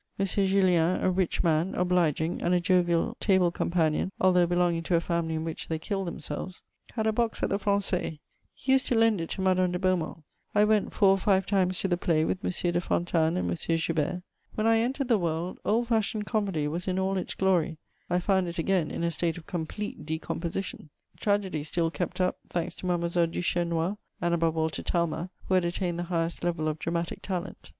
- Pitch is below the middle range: No, medium, 180 Hz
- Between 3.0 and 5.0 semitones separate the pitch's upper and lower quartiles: No, narrow, 2.5 semitones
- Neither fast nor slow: No, fast, 210 wpm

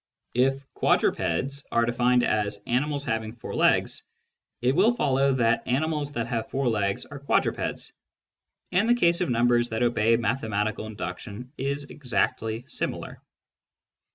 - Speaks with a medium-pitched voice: No, low, 125 Hz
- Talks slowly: No, average, 145 wpm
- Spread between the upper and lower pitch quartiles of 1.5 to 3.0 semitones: No, average, 3.8 semitones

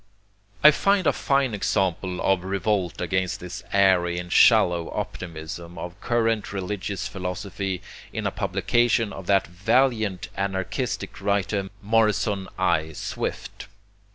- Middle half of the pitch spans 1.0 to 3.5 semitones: Yes, average, 2.9 semitones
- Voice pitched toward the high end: No, very low, 95 Hz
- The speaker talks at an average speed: No, slow, 120 wpm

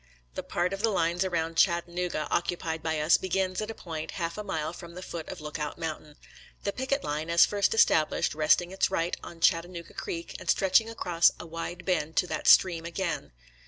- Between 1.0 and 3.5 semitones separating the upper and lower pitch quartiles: Yes, narrow, 2.4 semitones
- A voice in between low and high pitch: Yes, medium, 170 Hz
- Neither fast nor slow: No, fast, 220 wpm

